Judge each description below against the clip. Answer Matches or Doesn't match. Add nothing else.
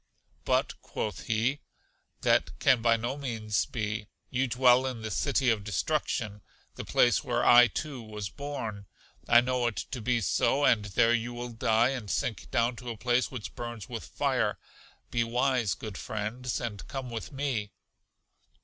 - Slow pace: Doesn't match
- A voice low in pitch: Matches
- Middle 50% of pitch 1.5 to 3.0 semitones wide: Matches